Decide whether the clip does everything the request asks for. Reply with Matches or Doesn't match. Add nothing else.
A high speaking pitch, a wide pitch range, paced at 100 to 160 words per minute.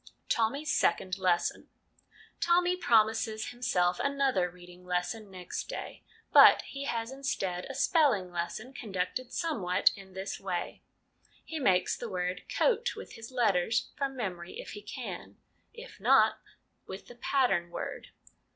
Matches